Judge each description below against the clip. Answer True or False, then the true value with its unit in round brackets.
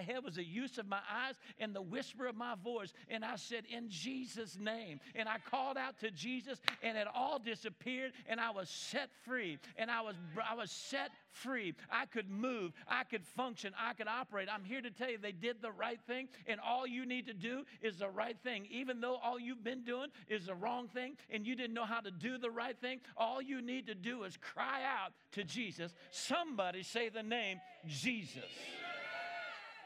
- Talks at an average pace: False (210 wpm)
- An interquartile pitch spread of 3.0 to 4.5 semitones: False (2.6 semitones)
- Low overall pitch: False (235 Hz)